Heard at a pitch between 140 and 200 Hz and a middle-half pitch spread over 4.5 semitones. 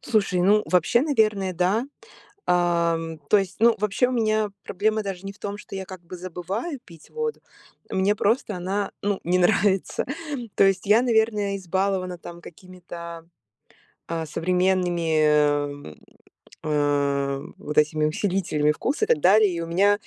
No: medium, 185 Hz; average, 3.6 semitones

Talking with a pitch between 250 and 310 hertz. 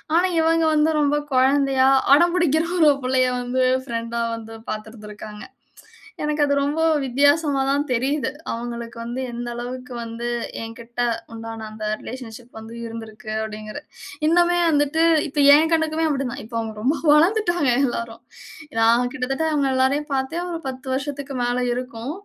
Yes: very high, 260 Hz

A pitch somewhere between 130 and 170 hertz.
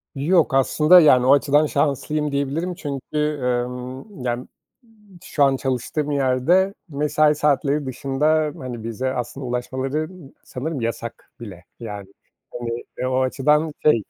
Yes: medium, 140 Hz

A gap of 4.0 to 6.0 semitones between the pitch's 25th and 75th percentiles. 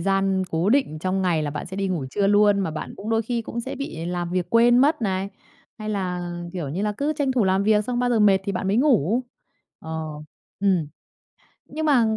Yes: average, 4.4 semitones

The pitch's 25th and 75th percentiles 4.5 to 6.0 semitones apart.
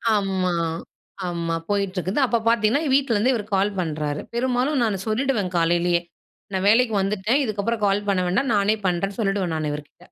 No: average, 4.1 semitones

